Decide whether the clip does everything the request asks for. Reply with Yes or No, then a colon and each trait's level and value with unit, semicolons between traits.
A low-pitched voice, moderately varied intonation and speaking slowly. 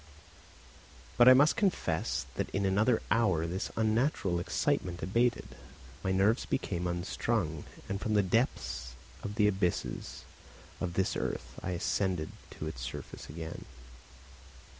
Yes: very low, 95 Hz; average, 4.5 semitones; slow, 130 wpm